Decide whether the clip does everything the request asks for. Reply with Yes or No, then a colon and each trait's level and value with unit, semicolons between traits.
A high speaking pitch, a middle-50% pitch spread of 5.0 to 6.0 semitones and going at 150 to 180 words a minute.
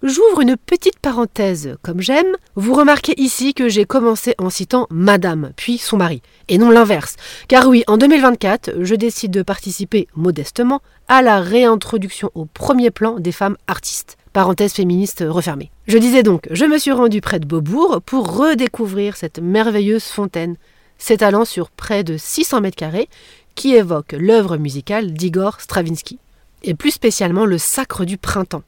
Yes: high, 210 Hz; wide, 5.4 semitones; average, 160 wpm